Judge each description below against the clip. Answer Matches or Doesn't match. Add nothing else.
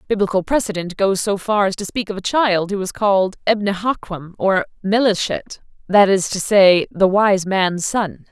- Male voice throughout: Doesn't match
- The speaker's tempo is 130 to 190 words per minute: Matches